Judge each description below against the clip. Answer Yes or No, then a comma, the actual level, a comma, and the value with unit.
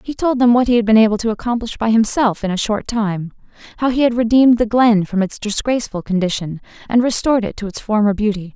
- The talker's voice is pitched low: No, high, 220 Hz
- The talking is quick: Yes, fast, 230 wpm